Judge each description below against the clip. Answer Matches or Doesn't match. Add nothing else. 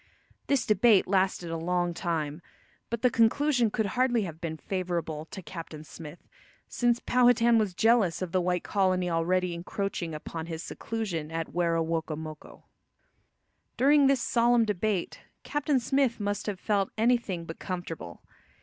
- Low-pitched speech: Doesn't match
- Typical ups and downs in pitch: Doesn't match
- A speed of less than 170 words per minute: Matches